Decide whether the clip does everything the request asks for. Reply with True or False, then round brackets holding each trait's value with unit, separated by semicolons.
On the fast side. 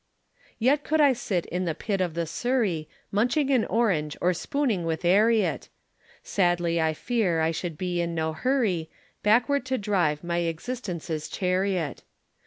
False (155 wpm)